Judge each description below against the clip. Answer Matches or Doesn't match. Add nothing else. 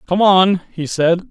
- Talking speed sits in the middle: Matches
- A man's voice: Matches